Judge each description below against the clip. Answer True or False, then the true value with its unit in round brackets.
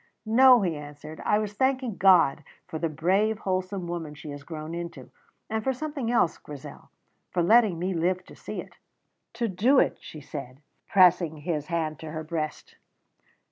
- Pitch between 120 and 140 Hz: False (175 Hz)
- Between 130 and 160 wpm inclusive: False (175 wpm)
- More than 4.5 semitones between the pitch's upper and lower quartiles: True (5.2 semitones)